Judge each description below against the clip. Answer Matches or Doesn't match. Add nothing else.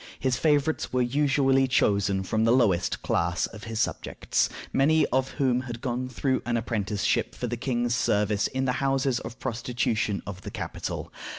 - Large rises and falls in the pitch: Doesn't match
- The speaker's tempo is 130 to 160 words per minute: Doesn't match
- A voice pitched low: Matches